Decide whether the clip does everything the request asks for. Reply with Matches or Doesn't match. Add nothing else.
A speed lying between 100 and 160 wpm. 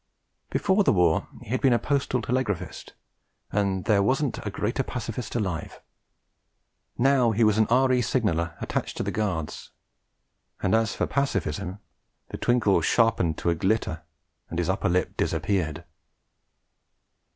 Matches